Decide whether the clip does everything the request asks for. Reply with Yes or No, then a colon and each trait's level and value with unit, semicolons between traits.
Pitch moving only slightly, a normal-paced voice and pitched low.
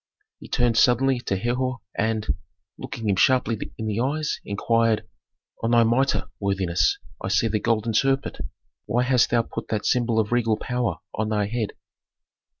Yes: narrow, 2.3 semitones; average, 160 wpm; low, 115 Hz